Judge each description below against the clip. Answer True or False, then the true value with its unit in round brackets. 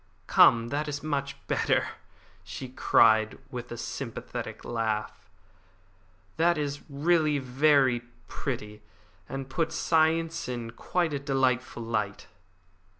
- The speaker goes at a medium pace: False (110 wpm)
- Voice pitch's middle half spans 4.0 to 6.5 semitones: True (4.4 semitones)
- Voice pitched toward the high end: False (135 Hz)